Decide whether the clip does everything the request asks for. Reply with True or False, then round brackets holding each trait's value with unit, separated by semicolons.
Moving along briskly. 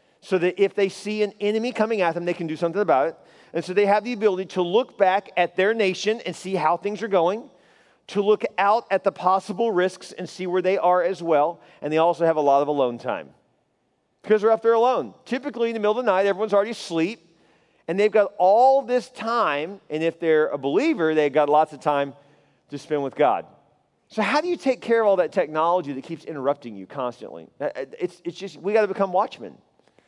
True (225 wpm)